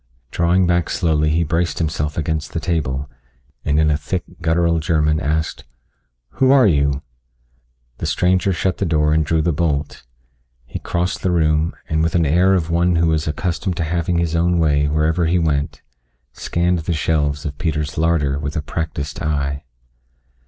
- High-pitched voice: No, very low, 80 Hz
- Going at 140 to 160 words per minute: No, average, 175 wpm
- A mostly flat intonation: Yes, narrow, 2.2 semitones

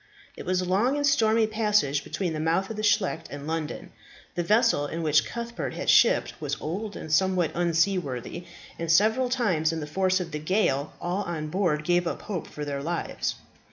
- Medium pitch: Yes, medium, 175 Hz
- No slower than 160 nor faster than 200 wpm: Yes, average, 195 wpm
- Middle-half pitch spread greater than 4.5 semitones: Yes, average, 5.0 semitones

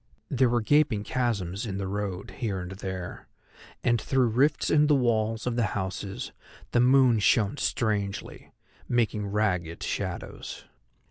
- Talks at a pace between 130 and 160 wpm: Yes, average, 140 wpm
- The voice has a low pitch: Yes, low, 110 Hz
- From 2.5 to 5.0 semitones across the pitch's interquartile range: Yes, average, 3.8 semitones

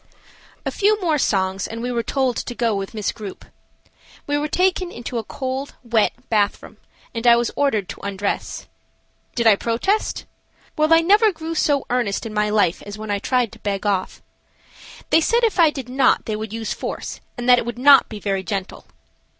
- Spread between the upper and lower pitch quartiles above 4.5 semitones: Yes, wide, 5.6 semitones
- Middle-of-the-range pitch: No, high, 235 Hz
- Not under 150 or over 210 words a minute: Yes, average, 200 wpm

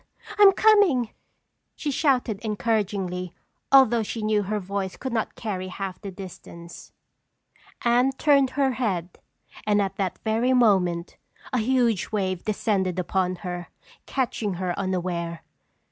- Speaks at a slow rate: Yes, slow, 130 wpm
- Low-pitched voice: No, high, 210 Hz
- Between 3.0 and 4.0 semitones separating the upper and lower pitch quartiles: No, average, 4.7 semitones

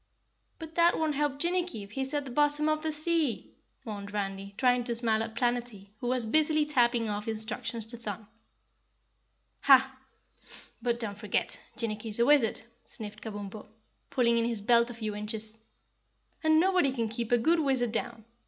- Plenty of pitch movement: No, average, 4.7 semitones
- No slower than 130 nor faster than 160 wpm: No, average, 170 wpm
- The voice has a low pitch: No, high, 235 Hz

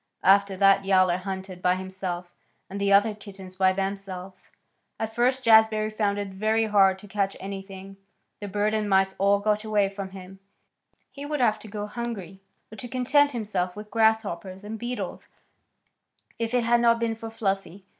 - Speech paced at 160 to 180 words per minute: Yes, average, 175 wpm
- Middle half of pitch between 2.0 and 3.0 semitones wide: Yes, narrow, 2.4 semitones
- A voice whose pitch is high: Yes, high, 200 Hz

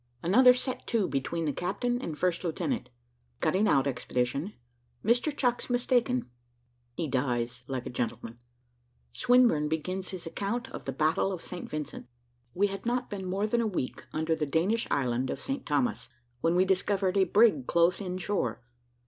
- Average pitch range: No, wide, 7.3 semitones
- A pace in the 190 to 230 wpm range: No, average, 165 wpm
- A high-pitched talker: No, medium, 180 Hz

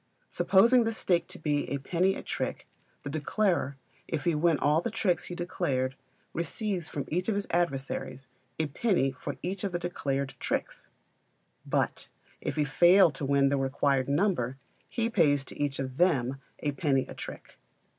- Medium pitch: Yes, medium, 155 Hz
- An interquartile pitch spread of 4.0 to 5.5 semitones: Yes, average, 4.7 semitones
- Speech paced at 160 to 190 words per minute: Yes, average, 175 wpm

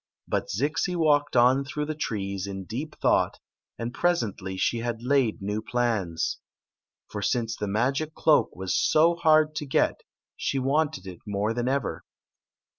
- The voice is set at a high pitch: No, low, 120 Hz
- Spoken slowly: No, average, 155 wpm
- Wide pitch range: Yes, wide, 6.2 semitones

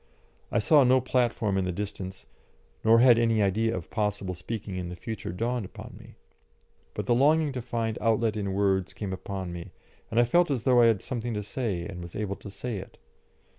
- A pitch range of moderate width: Yes, average, 3.9 semitones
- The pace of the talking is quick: Yes, fast, 210 wpm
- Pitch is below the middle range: Yes, low, 110 Hz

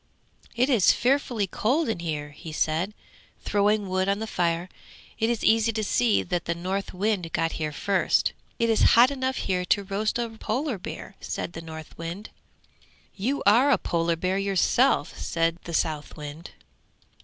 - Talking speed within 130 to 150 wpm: No, average, 160 wpm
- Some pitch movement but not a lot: Yes, average, 5.0 semitones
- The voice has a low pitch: No, high, 195 Hz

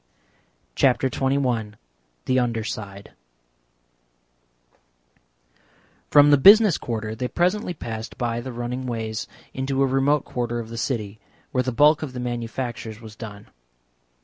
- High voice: No, low, 120 Hz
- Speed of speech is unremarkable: No, slow, 130 wpm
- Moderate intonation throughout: Yes, average, 3.1 semitones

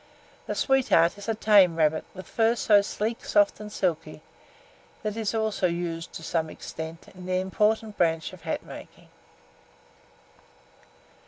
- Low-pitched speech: No, high, 190 Hz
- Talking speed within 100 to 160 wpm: Yes, average, 155 wpm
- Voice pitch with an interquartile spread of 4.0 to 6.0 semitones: Yes, average, 4.4 semitones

